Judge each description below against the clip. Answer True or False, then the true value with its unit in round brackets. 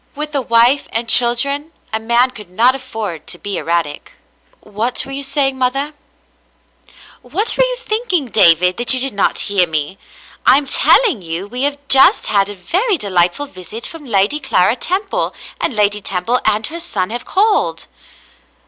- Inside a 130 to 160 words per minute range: False (175 wpm)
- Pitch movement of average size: False (6.1 semitones)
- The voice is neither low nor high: False (240 Hz)